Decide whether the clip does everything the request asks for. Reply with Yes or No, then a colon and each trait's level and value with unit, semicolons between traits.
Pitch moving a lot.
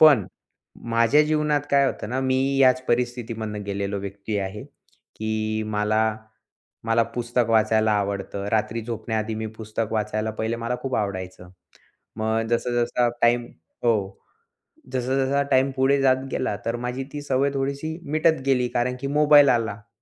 No: average, 3.5 semitones